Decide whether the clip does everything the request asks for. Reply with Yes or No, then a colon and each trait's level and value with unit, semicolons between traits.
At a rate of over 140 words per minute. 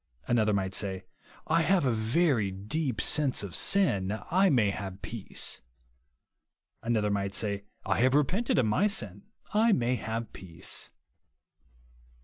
No: slow, 135 wpm